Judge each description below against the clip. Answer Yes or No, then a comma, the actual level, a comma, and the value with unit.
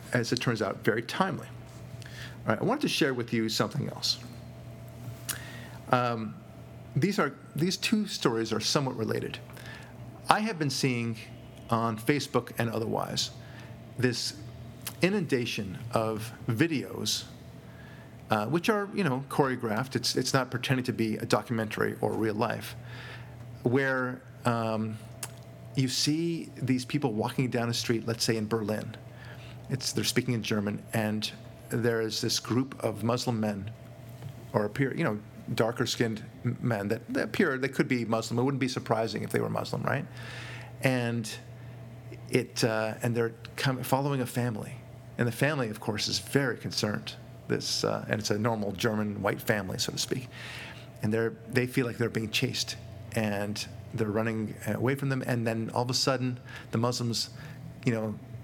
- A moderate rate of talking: Yes, average, 160 wpm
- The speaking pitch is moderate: No, low, 120 Hz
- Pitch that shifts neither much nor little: No, narrow, 2.2 semitones